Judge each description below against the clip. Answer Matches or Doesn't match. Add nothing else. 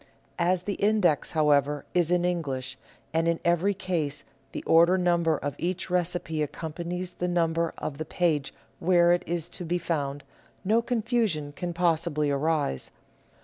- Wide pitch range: Doesn't match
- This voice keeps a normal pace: Matches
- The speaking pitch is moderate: Matches